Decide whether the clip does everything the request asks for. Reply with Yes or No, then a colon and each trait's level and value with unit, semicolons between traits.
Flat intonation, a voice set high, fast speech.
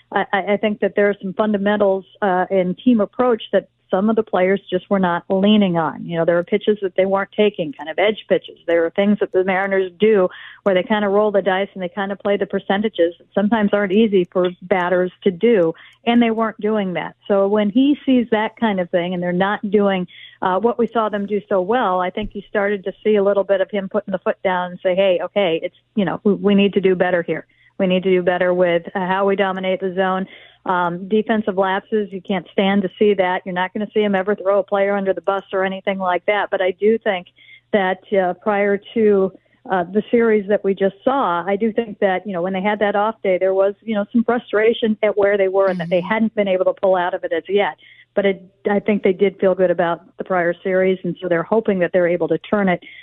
Yes: narrow, 2.1 semitones; high, 195 Hz; fast, 255 wpm